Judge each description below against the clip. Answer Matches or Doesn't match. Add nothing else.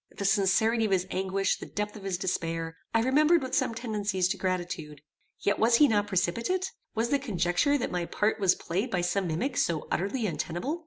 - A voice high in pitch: Matches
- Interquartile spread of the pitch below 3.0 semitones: Doesn't match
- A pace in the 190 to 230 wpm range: Matches